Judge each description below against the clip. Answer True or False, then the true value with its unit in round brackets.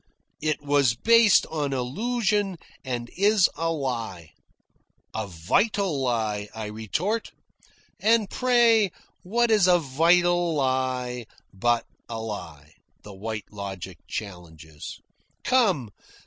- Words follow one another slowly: True (105 wpm)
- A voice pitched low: True (130 Hz)